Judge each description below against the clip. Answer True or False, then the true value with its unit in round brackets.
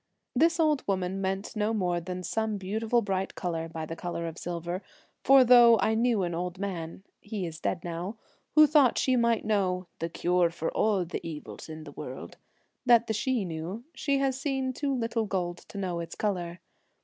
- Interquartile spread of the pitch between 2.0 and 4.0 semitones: False (5.1 semitones)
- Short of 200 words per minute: False (205 wpm)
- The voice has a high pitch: True (195 Hz)